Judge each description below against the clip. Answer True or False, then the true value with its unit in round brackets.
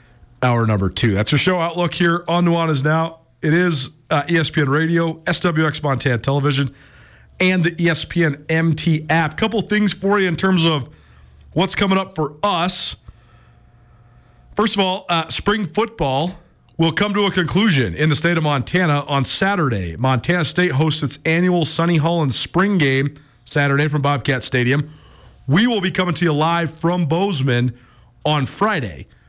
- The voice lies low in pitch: False (160 Hz)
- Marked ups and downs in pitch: False (4.3 semitones)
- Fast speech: False (160 wpm)